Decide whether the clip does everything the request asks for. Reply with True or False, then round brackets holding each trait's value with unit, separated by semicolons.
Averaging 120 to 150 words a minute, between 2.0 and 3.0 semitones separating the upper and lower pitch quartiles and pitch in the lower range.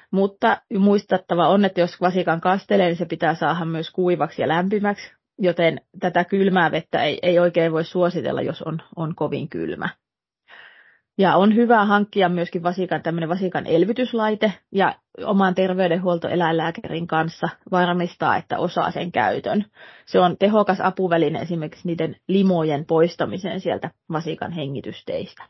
False (130 wpm; 2.6 semitones; 175 Hz)